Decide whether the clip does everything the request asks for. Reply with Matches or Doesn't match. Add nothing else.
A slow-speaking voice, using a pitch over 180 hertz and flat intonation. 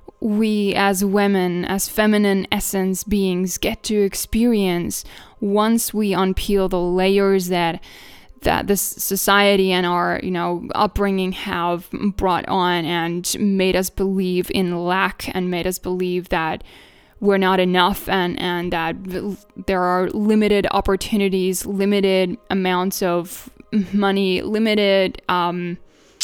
Matches